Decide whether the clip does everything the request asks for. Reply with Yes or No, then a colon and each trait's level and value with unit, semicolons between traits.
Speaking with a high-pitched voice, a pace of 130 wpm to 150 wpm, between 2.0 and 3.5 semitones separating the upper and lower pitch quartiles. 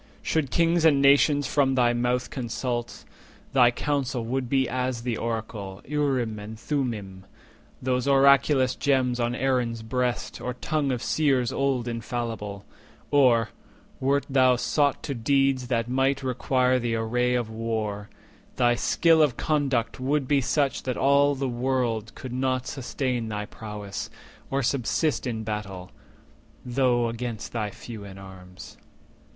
No: low, 125 Hz; average, 140 wpm; average, 2.9 semitones